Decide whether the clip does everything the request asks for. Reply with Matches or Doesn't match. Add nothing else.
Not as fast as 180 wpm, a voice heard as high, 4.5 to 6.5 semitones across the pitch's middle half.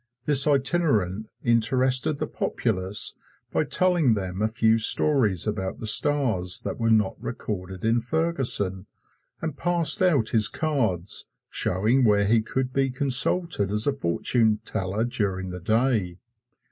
Doesn't match